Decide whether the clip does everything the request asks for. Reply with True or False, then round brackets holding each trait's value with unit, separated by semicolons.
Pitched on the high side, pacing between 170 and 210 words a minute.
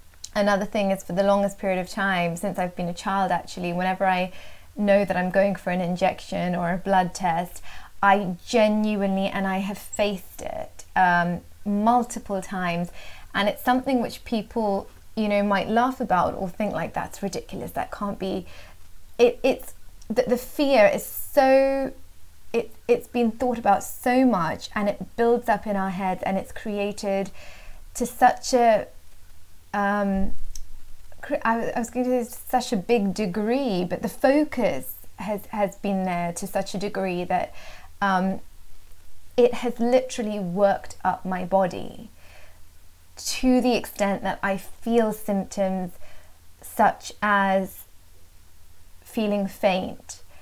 False (195 Hz; 150 wpm)